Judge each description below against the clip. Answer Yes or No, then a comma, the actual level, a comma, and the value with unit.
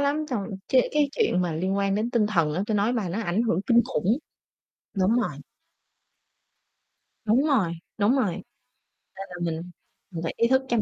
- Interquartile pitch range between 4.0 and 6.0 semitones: Yes, average, 5.1 semitones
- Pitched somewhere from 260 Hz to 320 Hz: No, high, 210 Hz